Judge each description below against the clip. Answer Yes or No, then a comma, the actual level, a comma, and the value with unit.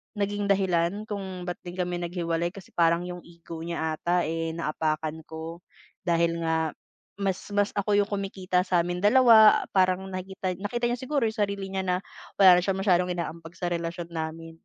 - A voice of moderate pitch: Yes, medium, 180 Hz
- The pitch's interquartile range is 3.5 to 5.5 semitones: No, average, 2.8 semitones